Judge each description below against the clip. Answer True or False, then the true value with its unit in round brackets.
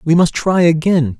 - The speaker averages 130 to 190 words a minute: False (200 wpm)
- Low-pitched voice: False (165 Hz)